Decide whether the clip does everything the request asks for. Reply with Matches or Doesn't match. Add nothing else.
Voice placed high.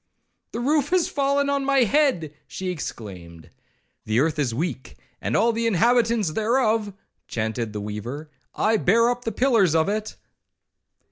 Matches